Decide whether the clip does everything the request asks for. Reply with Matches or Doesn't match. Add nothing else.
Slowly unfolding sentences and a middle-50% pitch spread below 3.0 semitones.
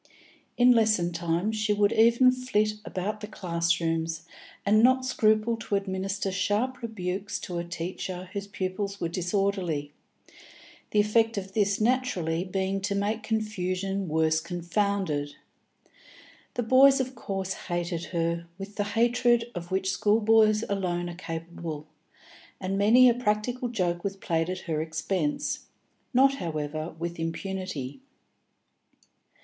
Doesn't match